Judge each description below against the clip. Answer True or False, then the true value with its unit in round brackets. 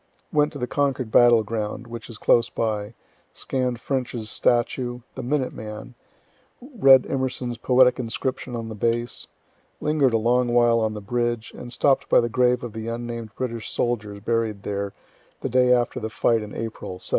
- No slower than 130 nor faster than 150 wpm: False (175 wpm)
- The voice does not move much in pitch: True (2.1 semitones)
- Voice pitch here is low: True (120 Hz)